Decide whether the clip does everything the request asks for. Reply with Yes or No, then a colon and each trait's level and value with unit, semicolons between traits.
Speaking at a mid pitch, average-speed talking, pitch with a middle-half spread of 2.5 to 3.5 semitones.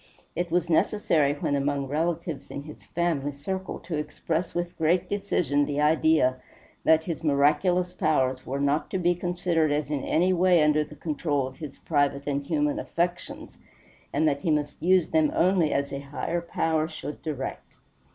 Yes: medium, 155 Hz; average, 170 wpm; average, 3.2 semitones